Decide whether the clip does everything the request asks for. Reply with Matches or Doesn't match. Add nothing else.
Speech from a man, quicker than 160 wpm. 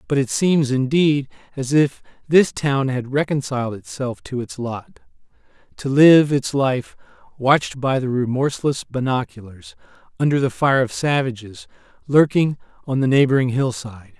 Doesn't match